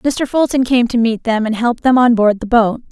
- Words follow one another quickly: Yes, fast, 265 wpm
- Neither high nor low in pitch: No, high, 235 Hz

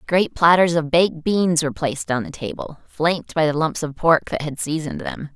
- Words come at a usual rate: No, fast, 225 wpm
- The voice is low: No, medium, 160 Hz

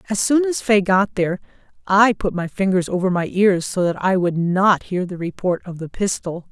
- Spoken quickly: Yes, fast, 220 wpm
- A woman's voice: Yes, female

